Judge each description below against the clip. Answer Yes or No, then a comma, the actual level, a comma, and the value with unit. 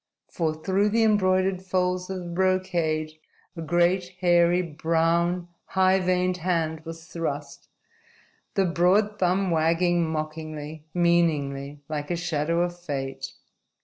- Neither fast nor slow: No, slow, 120 wpm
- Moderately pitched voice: Yes, medium, 175 Hz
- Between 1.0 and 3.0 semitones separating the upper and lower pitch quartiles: Yes, narrow, 2.4 semitones